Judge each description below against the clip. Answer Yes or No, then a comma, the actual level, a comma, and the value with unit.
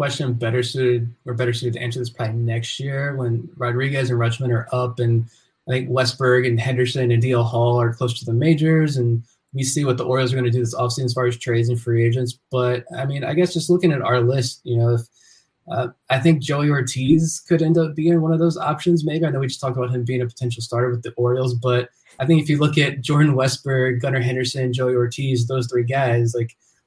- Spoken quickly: Yes, fast, 245 wpm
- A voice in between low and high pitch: No, low, 125 Hz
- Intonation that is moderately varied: No, narrow, 2.2 semitones